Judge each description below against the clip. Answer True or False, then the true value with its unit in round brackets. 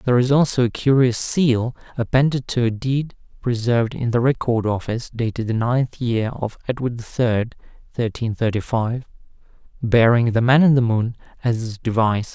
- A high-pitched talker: False (120 Hz)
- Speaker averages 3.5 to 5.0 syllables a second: True (4.9 syllables/s)